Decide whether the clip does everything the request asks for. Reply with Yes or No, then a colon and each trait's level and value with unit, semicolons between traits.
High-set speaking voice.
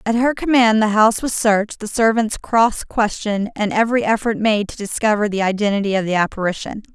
Yes: high, 215 Hz